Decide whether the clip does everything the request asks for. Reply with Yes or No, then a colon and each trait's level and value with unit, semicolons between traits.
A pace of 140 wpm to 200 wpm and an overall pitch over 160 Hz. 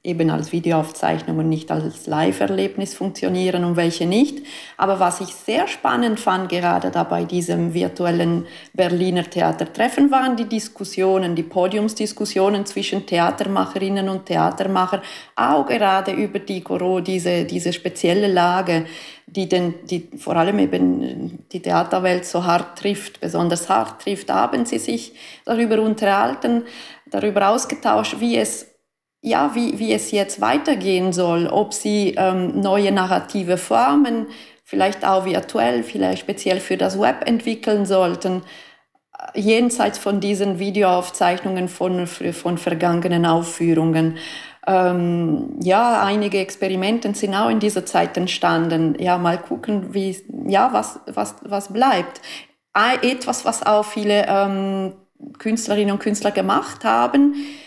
No: average, 130 wpm; high, 190 Hz